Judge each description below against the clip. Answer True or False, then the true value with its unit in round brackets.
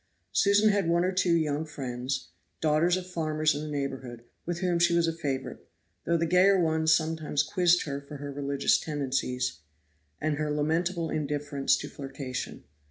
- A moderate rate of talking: True (165 wpm)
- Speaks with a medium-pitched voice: True (155 Hz)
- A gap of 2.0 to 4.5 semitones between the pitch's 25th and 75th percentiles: True (3.3 semitones)